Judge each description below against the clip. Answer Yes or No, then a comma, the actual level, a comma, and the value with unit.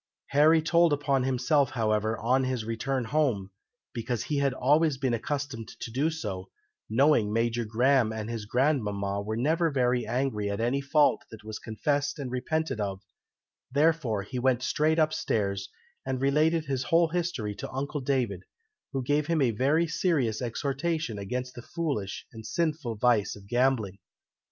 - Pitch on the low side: Yes, low, 130 Hz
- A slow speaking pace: No, average, 160 wpm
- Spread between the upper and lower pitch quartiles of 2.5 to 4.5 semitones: No, average, 4.9 semitones